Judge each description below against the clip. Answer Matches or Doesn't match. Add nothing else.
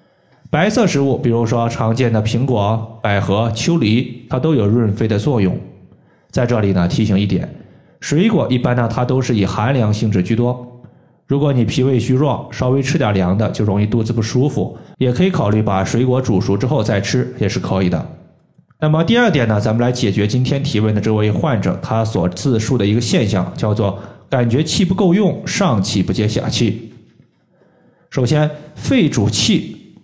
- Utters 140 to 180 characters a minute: Doesn't match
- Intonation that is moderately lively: Matches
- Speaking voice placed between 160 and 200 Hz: Doesn't match